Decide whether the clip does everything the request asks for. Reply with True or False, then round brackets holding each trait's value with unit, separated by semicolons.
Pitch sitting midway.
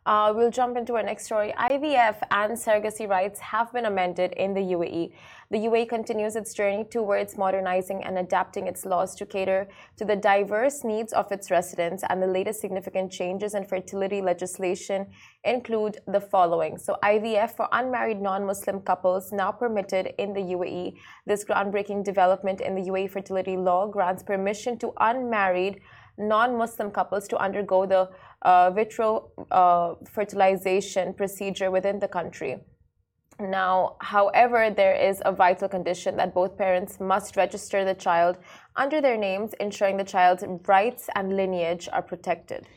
False (195 Hz)